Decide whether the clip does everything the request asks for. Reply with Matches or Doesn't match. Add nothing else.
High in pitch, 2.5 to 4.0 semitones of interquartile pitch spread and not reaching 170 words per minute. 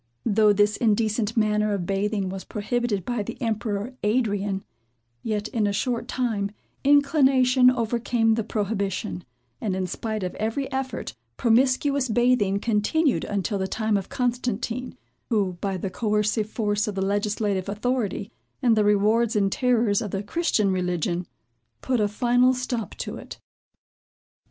Matches